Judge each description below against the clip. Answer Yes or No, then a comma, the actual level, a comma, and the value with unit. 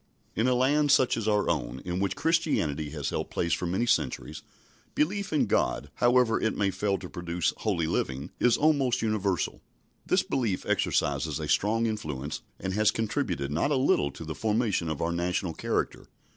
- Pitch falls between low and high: No, low, 100 Hz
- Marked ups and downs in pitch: Yes, wide, 6.8 semitones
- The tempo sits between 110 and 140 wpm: No, average, 180 wpm